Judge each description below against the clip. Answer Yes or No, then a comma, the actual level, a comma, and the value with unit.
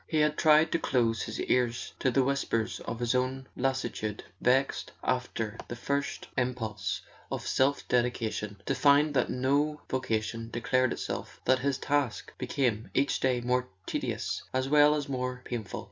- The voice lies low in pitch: Yes, low, 125 Hz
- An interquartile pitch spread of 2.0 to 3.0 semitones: Yes, average, 2.7 semitones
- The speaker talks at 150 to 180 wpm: Yes, average, 160 wpm